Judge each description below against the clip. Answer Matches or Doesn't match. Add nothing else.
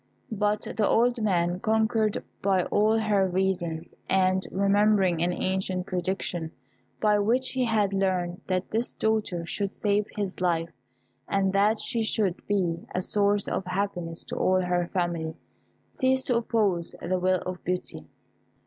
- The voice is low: Doesn't match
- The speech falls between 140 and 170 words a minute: Matches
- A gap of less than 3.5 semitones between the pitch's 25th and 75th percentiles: Matches